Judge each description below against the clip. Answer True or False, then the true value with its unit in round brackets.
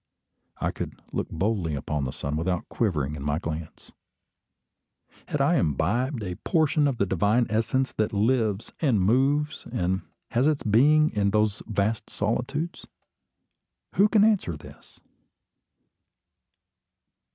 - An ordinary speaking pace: False (130 wpm)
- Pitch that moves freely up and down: True (6.7 semitones)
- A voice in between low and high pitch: False (110 Hz)